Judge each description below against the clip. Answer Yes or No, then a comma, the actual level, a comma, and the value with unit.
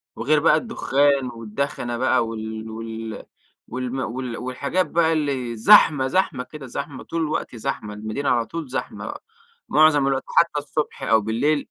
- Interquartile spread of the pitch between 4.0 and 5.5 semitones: Yes, average, 4.5 semitones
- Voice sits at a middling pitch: No, low, 130 Hz